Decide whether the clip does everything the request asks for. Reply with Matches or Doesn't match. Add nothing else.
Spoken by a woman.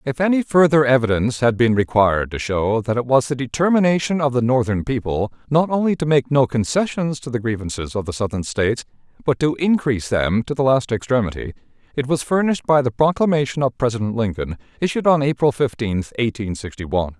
Doesn't match